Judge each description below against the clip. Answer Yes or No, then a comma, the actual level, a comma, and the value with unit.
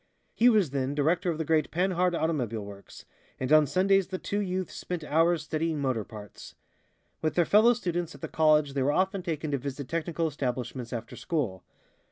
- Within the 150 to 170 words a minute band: No, average, 190 wpm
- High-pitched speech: No, medium, 155 Hz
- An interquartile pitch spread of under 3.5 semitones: No, average, 4.6 semitones